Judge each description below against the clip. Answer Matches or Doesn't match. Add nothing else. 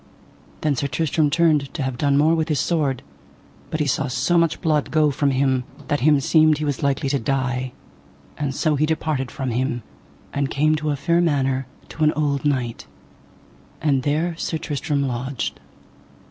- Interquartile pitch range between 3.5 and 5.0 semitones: Doesn't match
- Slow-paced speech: Doesn't match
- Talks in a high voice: Doesn't match